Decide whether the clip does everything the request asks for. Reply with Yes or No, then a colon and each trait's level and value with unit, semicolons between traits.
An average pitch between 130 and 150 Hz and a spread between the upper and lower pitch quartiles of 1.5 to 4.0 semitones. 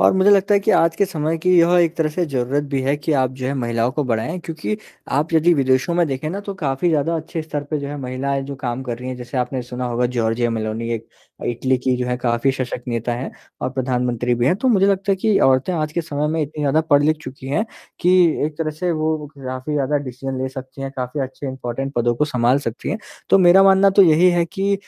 No: medium, 140 Hz; average, 4.7 semitones